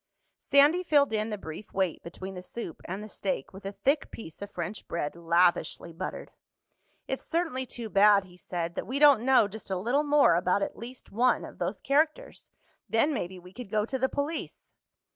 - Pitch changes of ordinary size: No, wide, 6.5 semitones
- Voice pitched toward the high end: Yes, high, 210 Hz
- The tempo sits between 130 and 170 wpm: No, average, 200 wpm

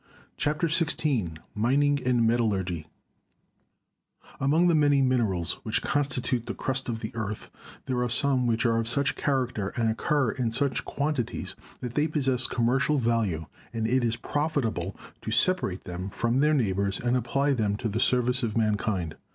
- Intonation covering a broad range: No, average, 4.0 semitones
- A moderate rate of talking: Yes, average, 160 wpm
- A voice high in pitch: No, low, 120 Hz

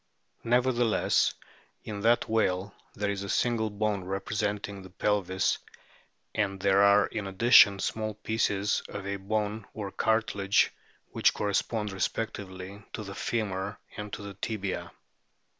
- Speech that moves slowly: Yes, slow, 130 wpm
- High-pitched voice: No, low, 100 Hz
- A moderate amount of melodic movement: No, narrow, 1.8 semitones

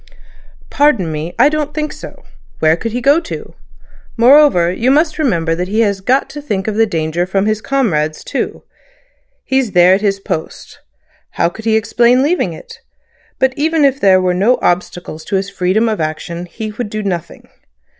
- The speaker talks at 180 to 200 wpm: Yes, average, 185 wpm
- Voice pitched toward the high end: Yes, high, 215 Hz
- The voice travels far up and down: Yes, wide, 6.9 semitones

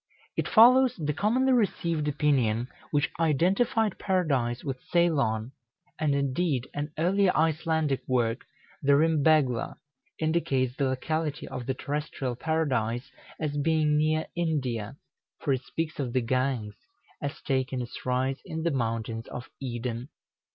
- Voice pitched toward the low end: No, medium, 145 Hz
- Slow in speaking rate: Yes, slow, 130 wpm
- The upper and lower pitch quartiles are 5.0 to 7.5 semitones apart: No, average, 4.1 semitones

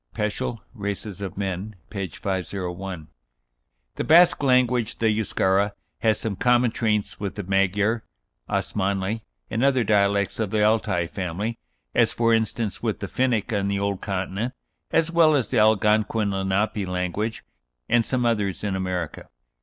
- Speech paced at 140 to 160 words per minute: Yes, average, 145 wpm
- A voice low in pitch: Yes, low, 105 Hz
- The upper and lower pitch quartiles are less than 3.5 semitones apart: Yes, average, 2.8 semitones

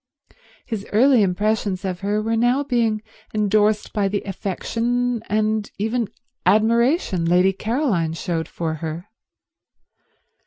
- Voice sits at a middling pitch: No, high, 215 Hz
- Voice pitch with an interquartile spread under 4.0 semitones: Yes, average, 3.2 semitones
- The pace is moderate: No, slow, 115 wpm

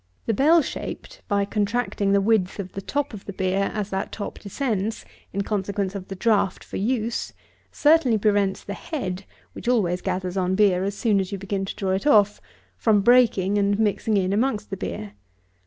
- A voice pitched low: No, high, 200 Hz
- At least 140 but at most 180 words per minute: No, average, 190 wpm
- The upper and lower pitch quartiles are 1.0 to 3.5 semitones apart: Yes, narrow, 2.6 semitones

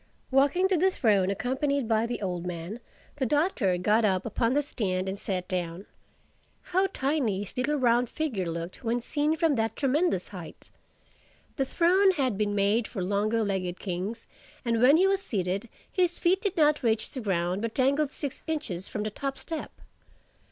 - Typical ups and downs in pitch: No, wide, 7.0 semitones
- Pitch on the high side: Yes, high, 230 Hz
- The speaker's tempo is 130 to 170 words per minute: No, average, 180 wpm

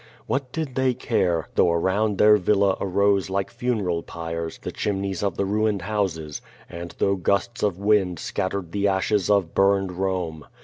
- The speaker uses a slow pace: No, average, 165 wpm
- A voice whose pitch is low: Yes, low, 100 Hz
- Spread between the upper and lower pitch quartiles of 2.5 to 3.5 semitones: Yes, average, 2.8 semitones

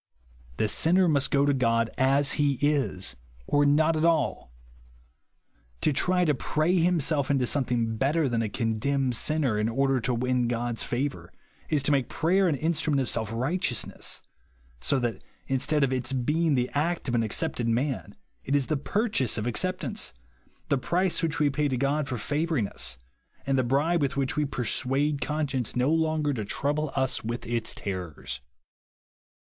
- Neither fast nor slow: Yes, average, 175 wpm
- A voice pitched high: No, low, 135 Hz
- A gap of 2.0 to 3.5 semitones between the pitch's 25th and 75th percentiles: No, average, 3.9 semitones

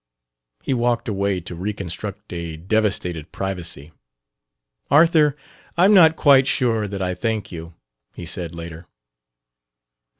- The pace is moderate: No, slow, 120 wpm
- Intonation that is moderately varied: No, wide, 5.8 semitones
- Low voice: Yes, low, 100 Hz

